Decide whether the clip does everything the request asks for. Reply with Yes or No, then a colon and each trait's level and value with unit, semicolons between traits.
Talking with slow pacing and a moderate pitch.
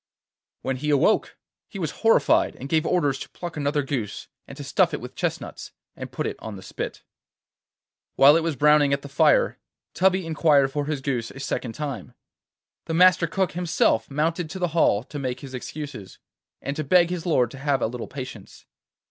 No: average, 190 wpm; medium, 145 Hz